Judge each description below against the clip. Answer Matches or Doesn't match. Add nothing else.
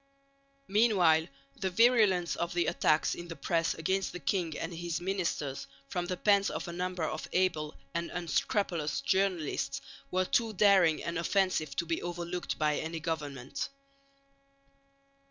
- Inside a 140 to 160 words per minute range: Matches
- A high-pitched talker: Doesn't match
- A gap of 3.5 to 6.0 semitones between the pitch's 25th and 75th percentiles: Doesn't match